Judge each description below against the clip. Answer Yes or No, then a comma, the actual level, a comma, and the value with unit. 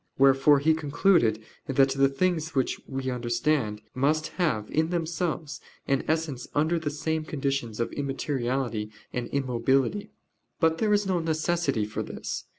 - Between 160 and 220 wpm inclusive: No, average, 145 wpm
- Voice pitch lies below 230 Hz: Yes, medium, 140 Hz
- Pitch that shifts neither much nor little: Yes, average, 3.6 semitones